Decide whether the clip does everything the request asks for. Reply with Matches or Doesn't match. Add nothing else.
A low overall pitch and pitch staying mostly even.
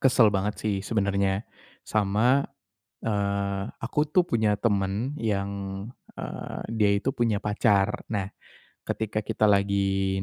Matches